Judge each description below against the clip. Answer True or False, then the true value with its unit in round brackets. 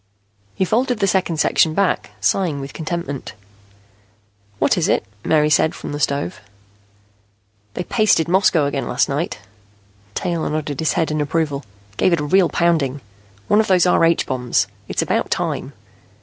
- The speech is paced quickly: False (160 wpm)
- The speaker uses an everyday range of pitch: True (3.9 semitones)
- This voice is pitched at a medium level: True (160 Hz)